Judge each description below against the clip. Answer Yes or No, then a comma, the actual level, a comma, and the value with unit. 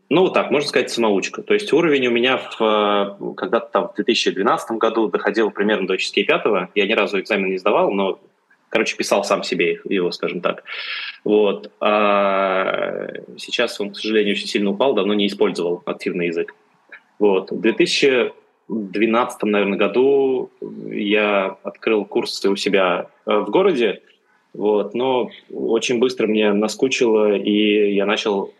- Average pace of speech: Yes, average, 150 wpm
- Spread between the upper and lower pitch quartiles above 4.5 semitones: Yes, average, 5.2 semitones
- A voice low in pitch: Yes, low, 110 Hz